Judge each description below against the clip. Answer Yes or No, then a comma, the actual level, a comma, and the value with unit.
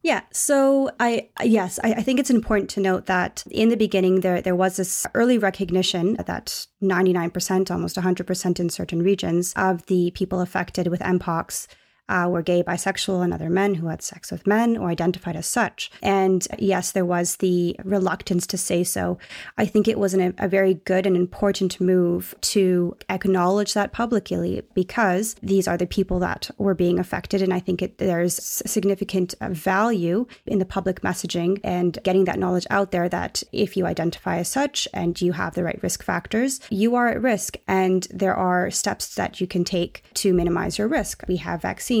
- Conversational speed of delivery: Yes, average, 190 wpm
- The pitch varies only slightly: Yes, narrow, 2.0 semitones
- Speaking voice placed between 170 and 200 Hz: Yes, medium, 185 Hz